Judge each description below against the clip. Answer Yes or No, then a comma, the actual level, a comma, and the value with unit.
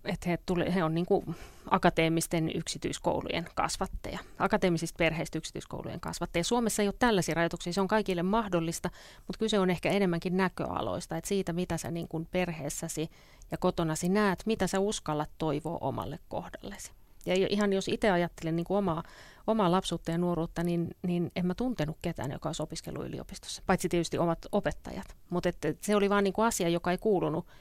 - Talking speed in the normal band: No, fast, 175 wpm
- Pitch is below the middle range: No, medium, 175 Hz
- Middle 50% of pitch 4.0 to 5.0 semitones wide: No, average, 2.8 semitones